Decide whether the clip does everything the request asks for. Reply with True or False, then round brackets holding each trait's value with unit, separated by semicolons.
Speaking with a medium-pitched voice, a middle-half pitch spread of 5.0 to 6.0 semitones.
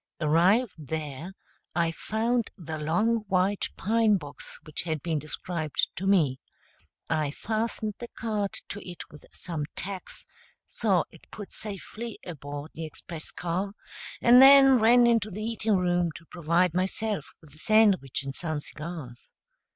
True (180 Hz; 5.5 semitones)